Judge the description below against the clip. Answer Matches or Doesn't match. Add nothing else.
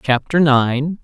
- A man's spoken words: Matches